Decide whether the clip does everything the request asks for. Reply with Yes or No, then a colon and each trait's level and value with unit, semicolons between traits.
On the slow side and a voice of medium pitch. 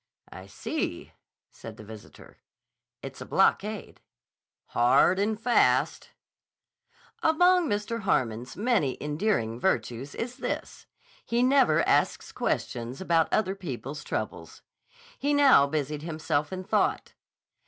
Yes: slow, 110 wpm; medium, 170 Hz